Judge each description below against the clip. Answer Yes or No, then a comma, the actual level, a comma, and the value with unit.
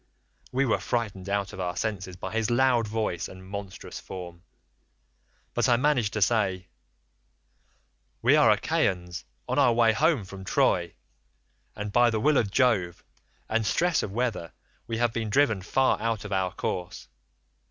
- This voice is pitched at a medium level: No, low, 105 Hz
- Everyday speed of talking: Yes, average, 160 wpm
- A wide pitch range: No, average, 4.1 semitones